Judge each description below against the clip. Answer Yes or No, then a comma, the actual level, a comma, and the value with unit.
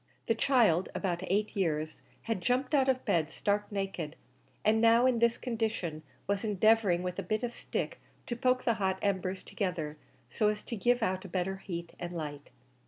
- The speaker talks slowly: No, average, 185 wpm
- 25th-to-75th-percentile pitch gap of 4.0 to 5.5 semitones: Yes, average, 4.4 semitones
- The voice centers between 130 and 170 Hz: No, high, 200 Hz